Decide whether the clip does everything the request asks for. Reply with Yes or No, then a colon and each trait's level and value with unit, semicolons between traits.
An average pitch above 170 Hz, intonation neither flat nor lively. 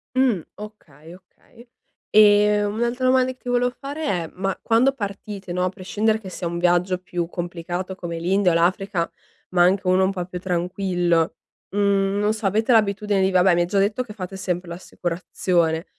Yes: high, 190 Hz; average, 3.0 semitones